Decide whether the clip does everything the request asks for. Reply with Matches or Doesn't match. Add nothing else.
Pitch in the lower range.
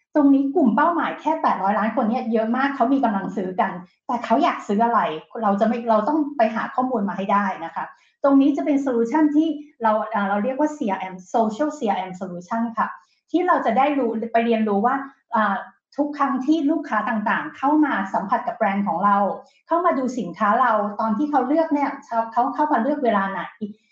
Doesn't match